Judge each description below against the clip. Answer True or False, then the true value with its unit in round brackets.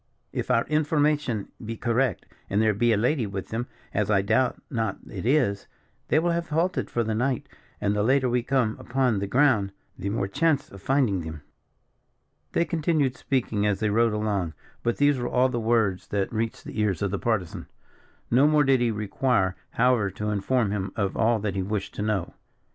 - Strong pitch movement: False (4.5 semitones)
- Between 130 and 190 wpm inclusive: False (200 wpm)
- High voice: False (115 Hz)